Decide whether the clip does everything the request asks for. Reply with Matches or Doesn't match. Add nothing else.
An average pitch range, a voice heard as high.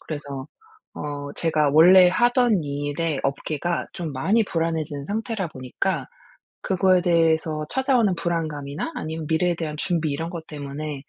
Doesn't match